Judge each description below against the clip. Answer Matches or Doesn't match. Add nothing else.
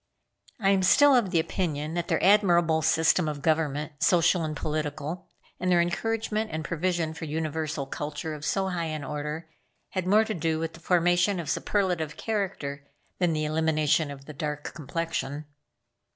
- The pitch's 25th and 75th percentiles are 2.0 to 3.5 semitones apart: Matches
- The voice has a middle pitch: Matches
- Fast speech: Doesn't match